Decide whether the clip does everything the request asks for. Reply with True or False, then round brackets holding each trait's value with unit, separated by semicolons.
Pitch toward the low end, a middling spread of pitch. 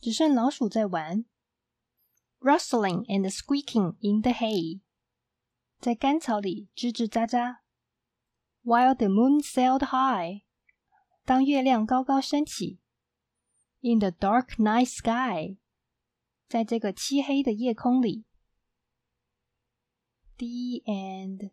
False (235 Hz; 4.7 semitones)